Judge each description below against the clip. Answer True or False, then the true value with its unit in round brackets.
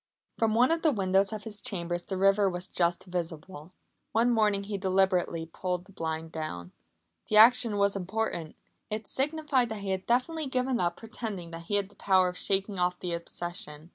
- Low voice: False (195 Hz)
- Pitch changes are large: False (4.0 semitones)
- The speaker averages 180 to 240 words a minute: True (190 wpm)